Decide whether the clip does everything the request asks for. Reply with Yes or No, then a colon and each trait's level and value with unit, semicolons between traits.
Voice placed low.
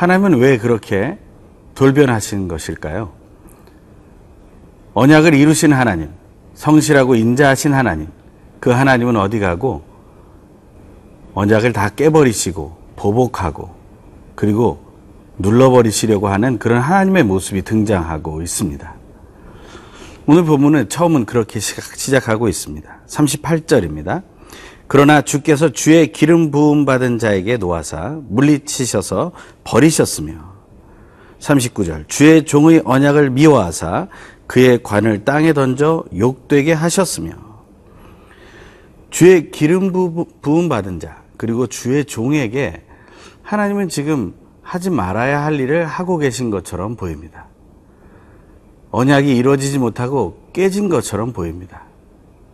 Yes: low, 125 Hz